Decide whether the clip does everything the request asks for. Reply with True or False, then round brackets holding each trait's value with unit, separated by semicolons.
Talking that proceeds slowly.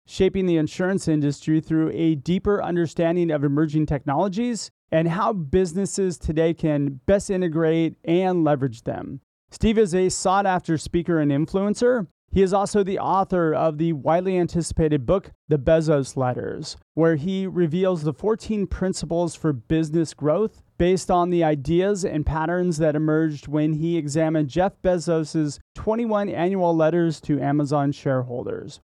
False (145 wpm)